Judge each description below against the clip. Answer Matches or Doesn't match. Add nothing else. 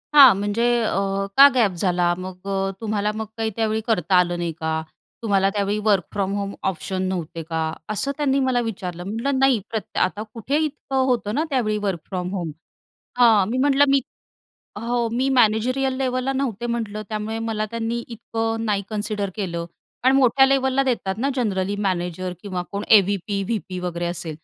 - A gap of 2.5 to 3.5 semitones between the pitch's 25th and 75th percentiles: Doesn't match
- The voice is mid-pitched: Doesn't match